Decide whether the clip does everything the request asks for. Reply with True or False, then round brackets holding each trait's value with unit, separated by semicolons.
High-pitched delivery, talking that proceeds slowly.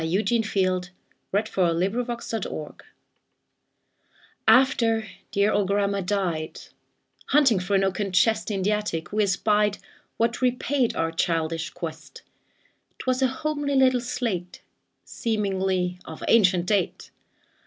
True (205 Hz; 115 wpm)